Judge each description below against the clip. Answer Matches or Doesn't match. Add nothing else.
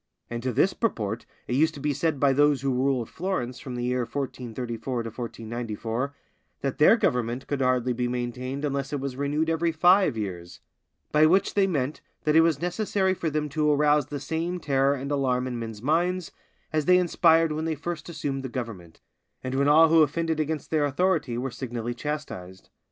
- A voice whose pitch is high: Doesn't match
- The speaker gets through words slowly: Doesn't match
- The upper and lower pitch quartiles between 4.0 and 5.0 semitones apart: Matches